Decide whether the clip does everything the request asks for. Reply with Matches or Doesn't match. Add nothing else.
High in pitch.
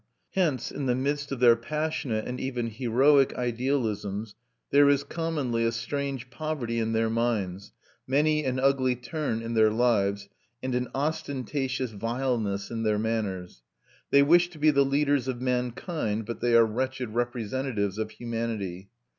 Doesn't match